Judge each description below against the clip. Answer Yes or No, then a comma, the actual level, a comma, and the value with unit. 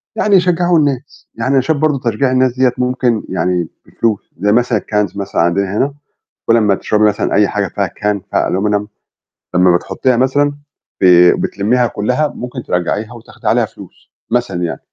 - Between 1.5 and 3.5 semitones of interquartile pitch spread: No, average, 4.5 semitones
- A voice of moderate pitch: No, low, 110 Hz